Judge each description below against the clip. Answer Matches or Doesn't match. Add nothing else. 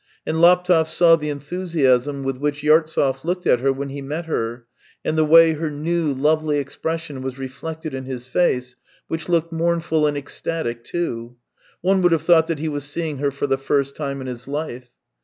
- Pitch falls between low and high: Matches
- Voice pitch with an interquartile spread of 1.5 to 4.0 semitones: Matches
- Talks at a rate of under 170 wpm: Doesn't match